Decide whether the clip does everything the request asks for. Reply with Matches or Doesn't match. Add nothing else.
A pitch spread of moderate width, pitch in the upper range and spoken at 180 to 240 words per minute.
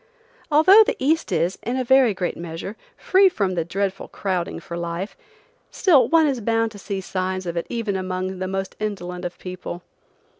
Matches